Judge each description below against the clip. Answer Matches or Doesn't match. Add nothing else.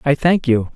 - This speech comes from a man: Matches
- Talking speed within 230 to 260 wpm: Matches